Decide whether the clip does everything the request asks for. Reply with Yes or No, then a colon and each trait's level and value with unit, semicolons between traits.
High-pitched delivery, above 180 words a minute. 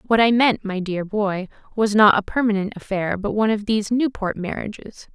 Yes: high, 210 Hz; average, 200 wpm